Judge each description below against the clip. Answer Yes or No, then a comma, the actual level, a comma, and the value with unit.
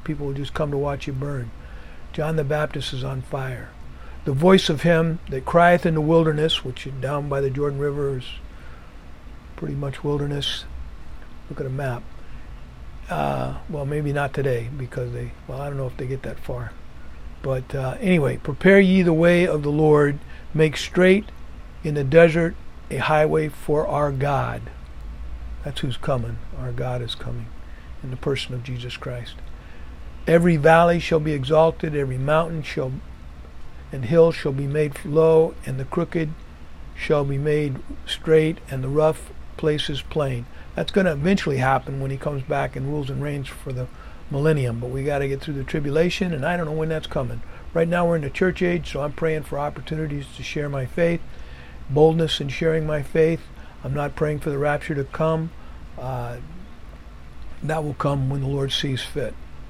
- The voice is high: No, medium, 140 Hz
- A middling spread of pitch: Yes, average, 4.2 semitones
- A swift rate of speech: No, average, 185 wpm